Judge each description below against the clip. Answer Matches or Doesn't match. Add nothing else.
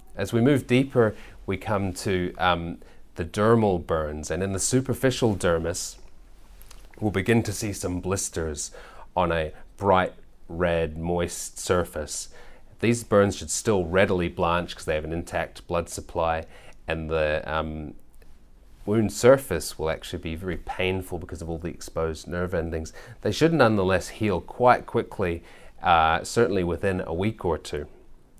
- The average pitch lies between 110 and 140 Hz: Doesn't match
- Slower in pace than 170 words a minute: Matches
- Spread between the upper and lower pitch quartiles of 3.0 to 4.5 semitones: Matches